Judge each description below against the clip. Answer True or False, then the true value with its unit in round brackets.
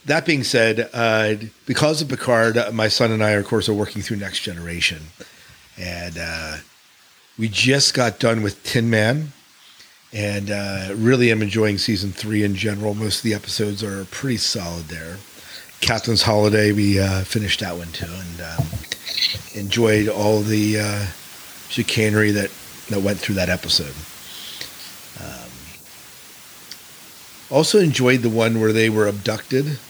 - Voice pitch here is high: False (105 Hz)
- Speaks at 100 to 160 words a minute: True (150 wpm)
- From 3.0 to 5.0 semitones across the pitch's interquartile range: False (2.6 semitones)